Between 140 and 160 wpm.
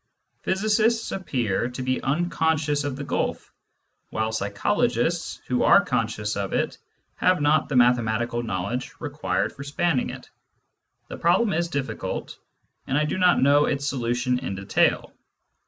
Yes: average, 145 wpm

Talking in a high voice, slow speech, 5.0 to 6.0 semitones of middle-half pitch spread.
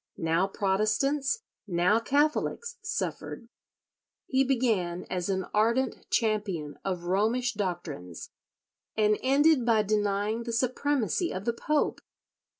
Yes: high, 215 Hz; slow, 110 wpm; wide, 5.5 semitones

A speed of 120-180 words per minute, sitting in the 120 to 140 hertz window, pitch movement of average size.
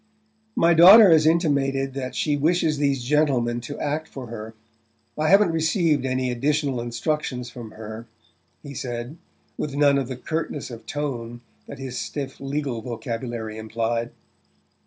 Yes: average, 145 wpm; low, 135 Hz; average, 4.1 semitones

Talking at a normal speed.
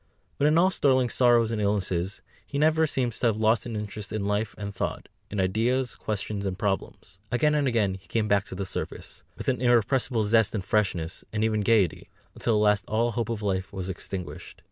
No: fast, 210 wpm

